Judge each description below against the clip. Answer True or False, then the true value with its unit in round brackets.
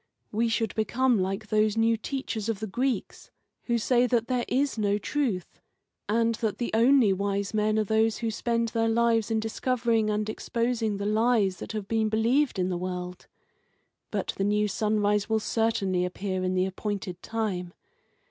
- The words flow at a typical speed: True (175 wpm)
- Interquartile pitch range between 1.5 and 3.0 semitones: True (2.4 semitones)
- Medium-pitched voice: False (220 Hz)